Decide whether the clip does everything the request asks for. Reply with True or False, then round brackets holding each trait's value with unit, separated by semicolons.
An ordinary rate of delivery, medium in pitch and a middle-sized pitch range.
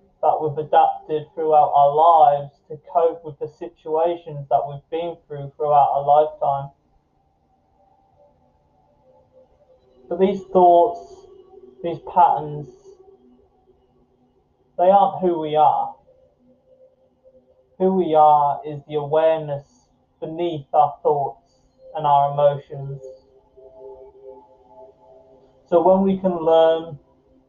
False (100 wpm; 155 Hz; 4.9 semitones)